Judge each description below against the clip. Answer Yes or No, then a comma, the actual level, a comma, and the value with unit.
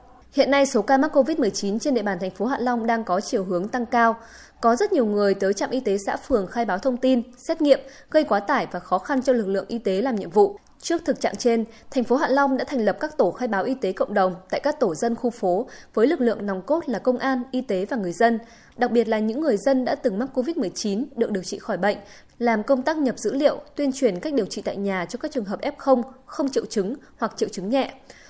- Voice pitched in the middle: No, high, 245 Hz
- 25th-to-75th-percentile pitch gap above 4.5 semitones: Yes, average, 4.9 semitones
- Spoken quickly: Yes, fast, 270 wpm